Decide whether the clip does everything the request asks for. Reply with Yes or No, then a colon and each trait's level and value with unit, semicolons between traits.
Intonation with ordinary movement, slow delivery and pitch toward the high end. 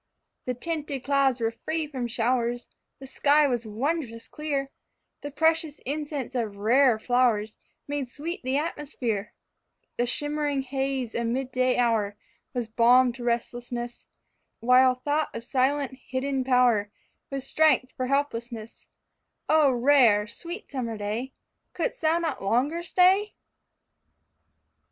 Yes: average, 3.4 semitones; slow, 130 wpm; very high, 255 Hz